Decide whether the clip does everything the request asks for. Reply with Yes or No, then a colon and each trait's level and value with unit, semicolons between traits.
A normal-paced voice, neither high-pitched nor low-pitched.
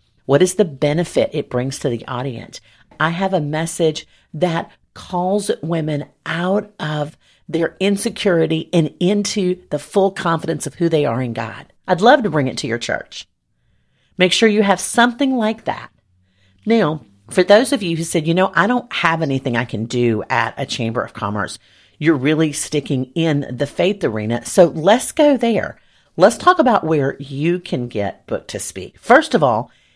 Yes: average, 180 wpm; medium, 160 Hz